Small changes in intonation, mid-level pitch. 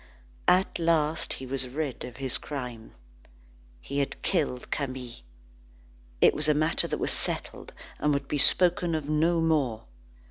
No: average, 3.4 semitones; medium, 145 Hz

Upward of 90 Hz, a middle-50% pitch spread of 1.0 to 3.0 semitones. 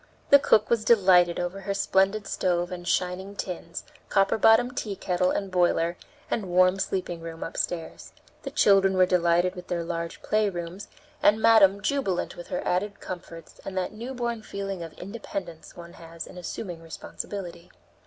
Yes: medium, 185 Hz; narrow, 2.6 semitones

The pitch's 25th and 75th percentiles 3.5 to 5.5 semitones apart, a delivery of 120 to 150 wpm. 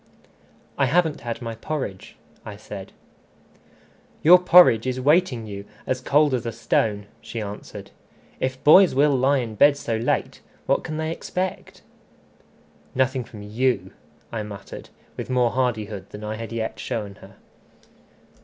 Yes: average, 4.7 semitones; average, 145 wpm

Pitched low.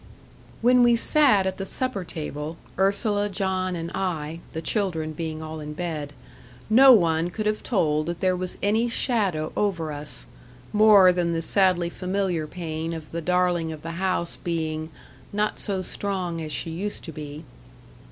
No: medium, 175 Hz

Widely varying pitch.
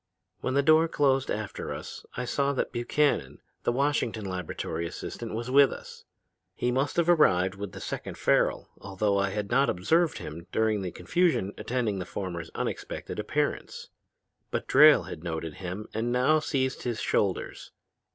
Yes: wide, 6.6 semitones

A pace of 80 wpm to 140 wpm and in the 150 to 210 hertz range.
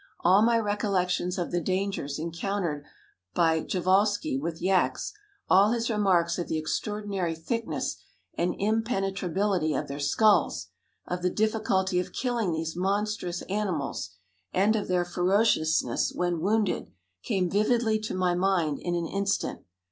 Yes: slow, 135 wpm; medium, 185 Hz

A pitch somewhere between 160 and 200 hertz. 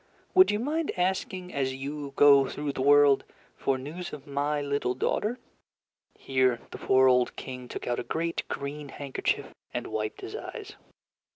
No: medium, 140 Hz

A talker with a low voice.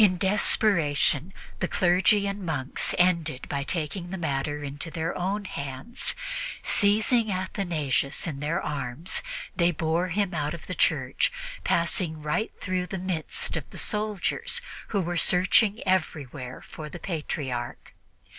No: medium, 170 Hz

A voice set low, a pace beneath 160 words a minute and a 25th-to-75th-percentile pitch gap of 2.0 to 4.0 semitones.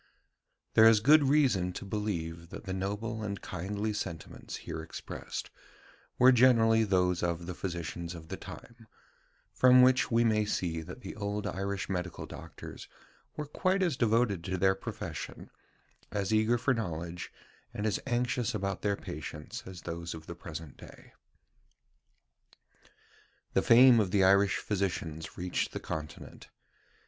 No: low, 100 Hz; average, 145 wpm; average, 4.6 semitones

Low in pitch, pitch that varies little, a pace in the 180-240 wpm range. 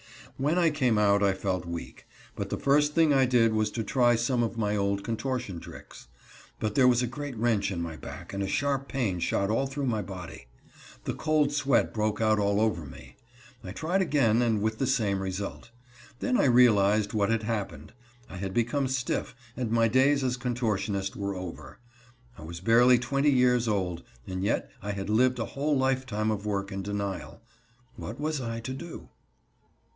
No: low, 115 Hz; average, 4.7 semitones; average, 190 wpm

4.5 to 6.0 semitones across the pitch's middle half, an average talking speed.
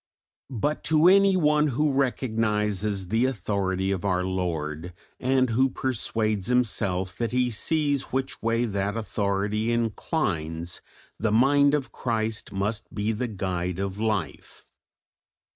No: average, 5.0 semitones; slow, 125 wpm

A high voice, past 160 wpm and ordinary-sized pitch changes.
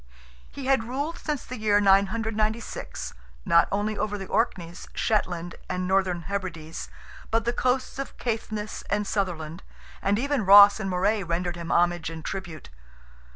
No: high, 200 Hz; average, 150 wpm; average, 4.0 semitones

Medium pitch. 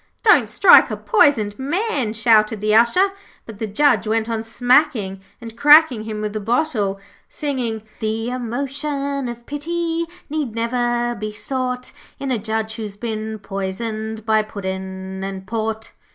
No: high, 225 Hz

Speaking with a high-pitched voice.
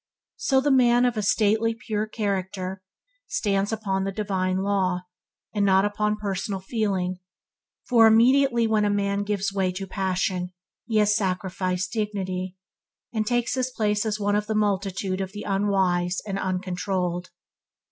Yes: high, 200 Hz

